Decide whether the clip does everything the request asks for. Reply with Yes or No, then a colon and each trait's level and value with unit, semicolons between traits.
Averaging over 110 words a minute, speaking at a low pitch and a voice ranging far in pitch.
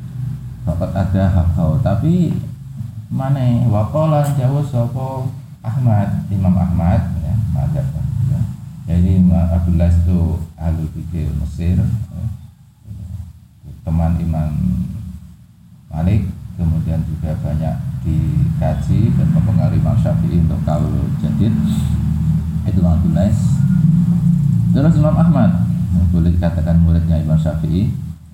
No: average, 105 wpm; very low, 95 Hz; wide, 7.4 semitones